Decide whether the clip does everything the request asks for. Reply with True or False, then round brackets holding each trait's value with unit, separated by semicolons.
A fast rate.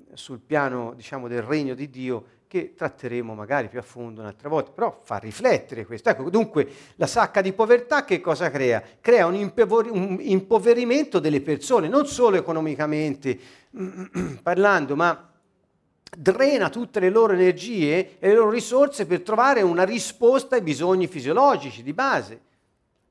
False (145 wpm)